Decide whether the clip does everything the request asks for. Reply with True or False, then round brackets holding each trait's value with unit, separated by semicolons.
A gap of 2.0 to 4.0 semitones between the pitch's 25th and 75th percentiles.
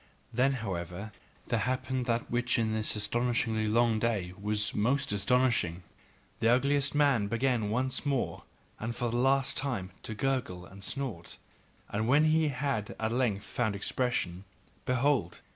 True (3.7 semitones)